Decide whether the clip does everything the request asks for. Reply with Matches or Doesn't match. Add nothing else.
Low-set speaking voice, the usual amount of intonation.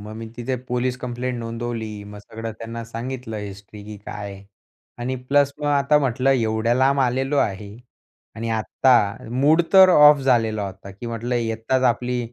Matches